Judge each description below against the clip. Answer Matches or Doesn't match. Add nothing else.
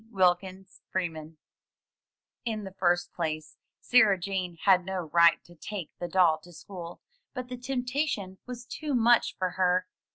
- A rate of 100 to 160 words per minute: Matches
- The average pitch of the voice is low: Doesn't match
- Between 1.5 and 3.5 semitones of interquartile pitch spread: Doesn't match